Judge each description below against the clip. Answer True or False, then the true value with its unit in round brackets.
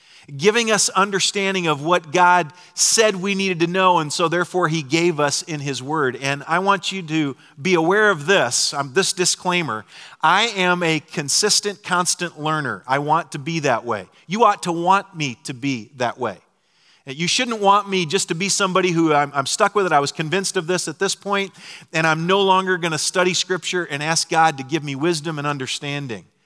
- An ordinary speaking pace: False (210 wpm)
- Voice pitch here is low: False (175 Hz)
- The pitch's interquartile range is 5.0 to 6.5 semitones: False (3.7 semitones)